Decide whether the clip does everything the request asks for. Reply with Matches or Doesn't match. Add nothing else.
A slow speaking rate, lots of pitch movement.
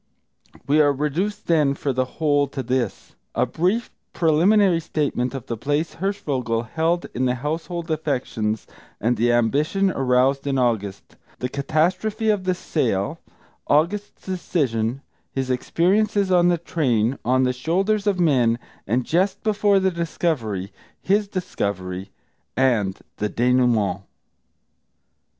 Matches